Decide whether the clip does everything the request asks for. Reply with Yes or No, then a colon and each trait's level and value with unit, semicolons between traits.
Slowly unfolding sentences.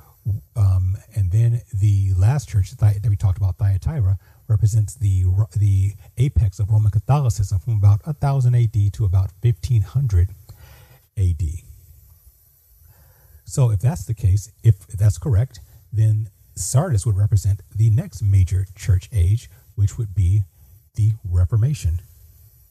Yes: slow, 125 wpm